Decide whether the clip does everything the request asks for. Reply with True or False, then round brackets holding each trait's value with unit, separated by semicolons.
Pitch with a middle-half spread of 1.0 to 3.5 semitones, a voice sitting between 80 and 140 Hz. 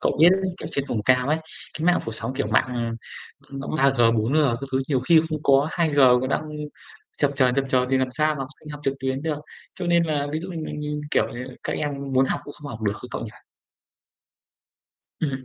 True (3.1 semitones; 135 Hz)